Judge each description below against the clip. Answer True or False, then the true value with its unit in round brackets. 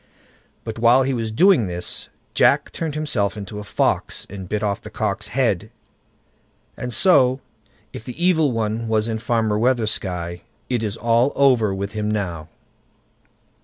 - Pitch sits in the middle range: False (110 Hz)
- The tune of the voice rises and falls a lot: False (3.4 semitones)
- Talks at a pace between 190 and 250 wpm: False (155 wpm)